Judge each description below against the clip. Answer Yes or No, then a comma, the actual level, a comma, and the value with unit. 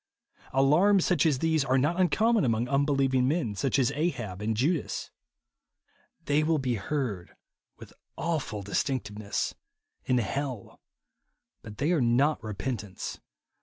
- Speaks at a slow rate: Yes, slow, 130 wpm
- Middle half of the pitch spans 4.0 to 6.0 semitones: Yes, average, 5.3 semitones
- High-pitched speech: No, low, 135 Hz